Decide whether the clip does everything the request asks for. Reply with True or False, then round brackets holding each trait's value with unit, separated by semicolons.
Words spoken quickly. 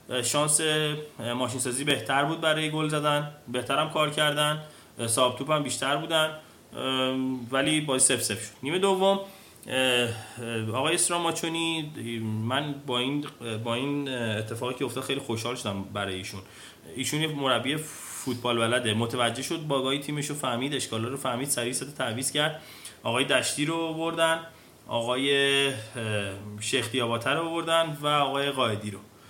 False (135 wpm)